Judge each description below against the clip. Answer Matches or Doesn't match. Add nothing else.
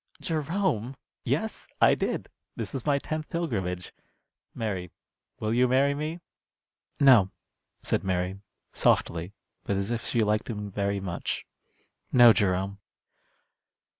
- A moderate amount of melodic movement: Doesn't match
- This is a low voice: Matches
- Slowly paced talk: Matches